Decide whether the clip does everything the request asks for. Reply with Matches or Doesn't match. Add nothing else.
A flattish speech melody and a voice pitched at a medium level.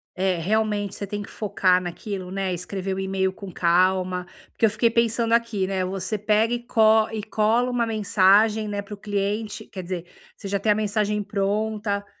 Doesn't match